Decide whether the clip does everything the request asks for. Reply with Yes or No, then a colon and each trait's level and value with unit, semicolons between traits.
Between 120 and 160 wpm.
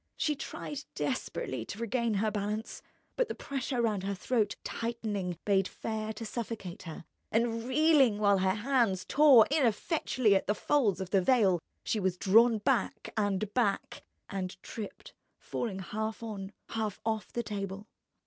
Yes: average, 155 wpm